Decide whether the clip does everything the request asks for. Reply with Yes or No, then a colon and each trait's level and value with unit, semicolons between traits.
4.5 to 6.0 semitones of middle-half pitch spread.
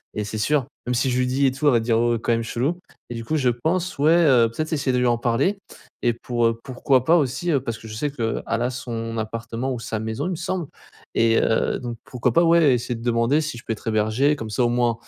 No: average, 3.5 semitones